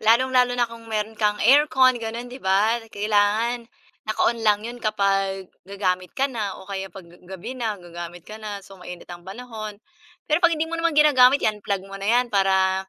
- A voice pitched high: Yes, high, 215 Hz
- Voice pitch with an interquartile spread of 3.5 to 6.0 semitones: Yes, average, 3.9 semitones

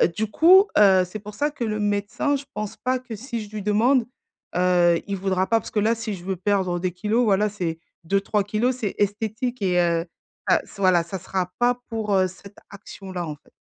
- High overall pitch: Yes, high, 205 Hz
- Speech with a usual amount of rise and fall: Yes, average, 3.2 semitones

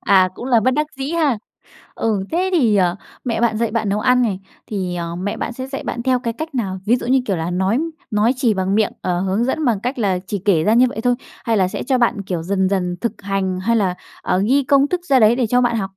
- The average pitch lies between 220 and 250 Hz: Yes, high, 225 Hz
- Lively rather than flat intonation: No, average, 4.6 semitones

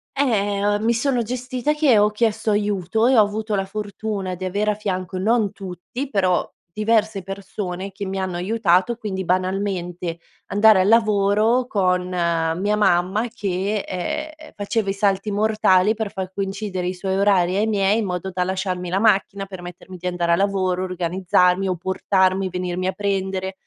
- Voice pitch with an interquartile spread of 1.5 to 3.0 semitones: Yes, narrow, 2.5 semitones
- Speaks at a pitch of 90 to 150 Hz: No, high, 195 Hz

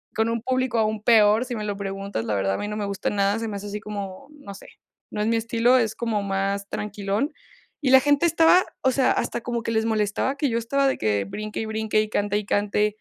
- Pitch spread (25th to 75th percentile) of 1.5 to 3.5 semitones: Yes, average, 2.7 semitones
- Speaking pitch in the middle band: No, high, 215 Hz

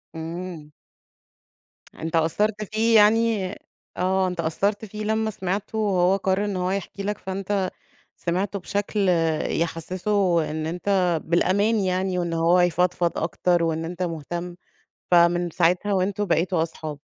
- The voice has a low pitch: No, medium, 185 Hz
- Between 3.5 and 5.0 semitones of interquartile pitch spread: No, average, 2.9 semitones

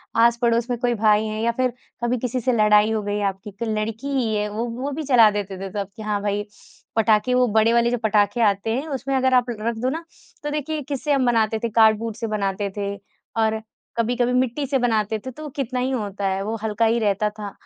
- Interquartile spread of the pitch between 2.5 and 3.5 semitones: Yes, average, 3.0 semitones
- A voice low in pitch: No, high, 225 Hz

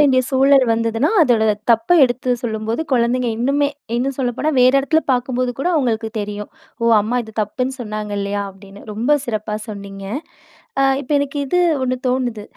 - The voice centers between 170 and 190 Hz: No, high, 245 Hz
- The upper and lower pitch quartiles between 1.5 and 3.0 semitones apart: No, average, 3.4 semitones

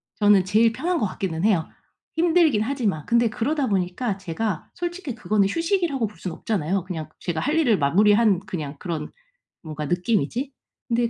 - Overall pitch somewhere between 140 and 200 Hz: No, high, 210 Hz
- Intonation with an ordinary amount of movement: No, wide, 6.0 semitones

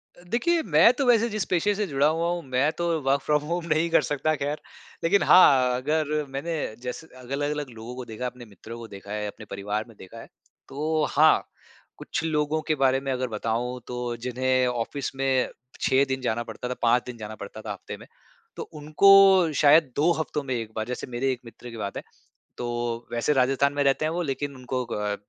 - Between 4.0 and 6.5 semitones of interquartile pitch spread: Yes, average, 4.3 semitones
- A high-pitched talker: No, low, 135 Hz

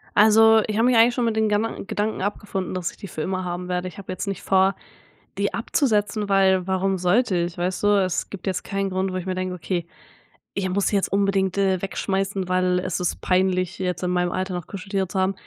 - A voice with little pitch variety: Yes, narrow, 1.7 semitones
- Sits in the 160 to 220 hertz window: Yes, high, 190 Hz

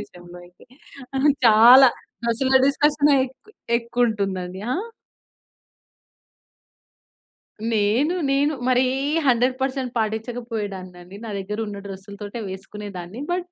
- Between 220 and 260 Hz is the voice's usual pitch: Yes, high, 225 Hz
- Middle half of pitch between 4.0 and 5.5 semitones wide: Yes, average, 4.6 semitones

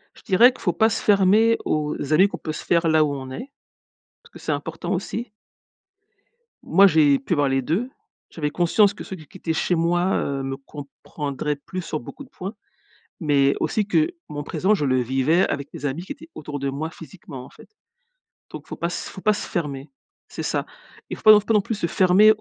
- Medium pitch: Yes, medium, 165 Hz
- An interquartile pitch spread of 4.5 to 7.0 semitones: Yes, wide, 5.6 semitones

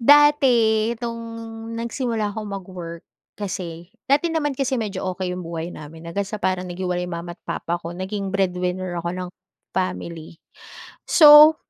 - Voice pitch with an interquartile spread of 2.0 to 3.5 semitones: No, average, 4.9 semitones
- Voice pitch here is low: No, high, 190 Hz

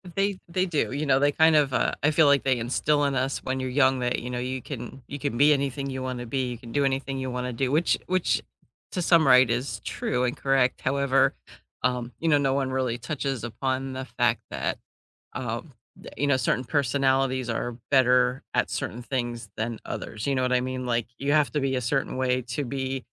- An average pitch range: No, narrow, 2.0 semitones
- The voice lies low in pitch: Yes, low, 130 Hz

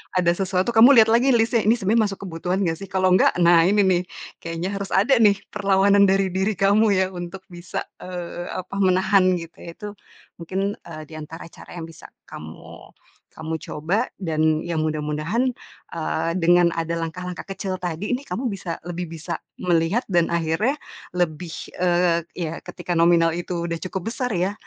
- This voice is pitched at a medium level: Yes, medium, 180 Hz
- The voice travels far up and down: No, average, 2.9 semitones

